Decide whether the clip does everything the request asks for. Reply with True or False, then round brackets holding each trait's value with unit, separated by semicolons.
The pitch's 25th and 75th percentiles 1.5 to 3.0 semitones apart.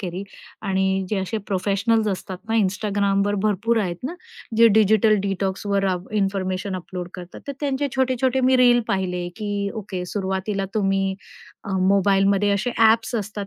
True (2.4 semitones)